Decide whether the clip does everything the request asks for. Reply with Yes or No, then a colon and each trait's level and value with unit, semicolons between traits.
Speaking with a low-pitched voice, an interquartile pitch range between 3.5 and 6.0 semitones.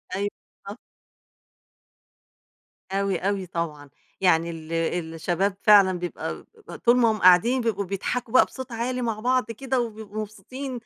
No: high, 205 Hz; average, 4.5 semitones